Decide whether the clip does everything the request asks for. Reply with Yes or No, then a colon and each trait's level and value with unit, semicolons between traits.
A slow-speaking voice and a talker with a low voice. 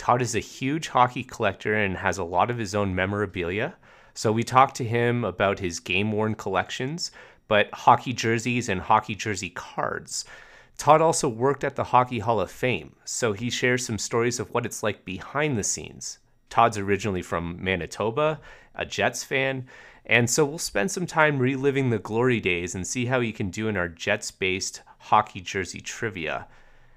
No: average, 180 wpm; low, 115 Hz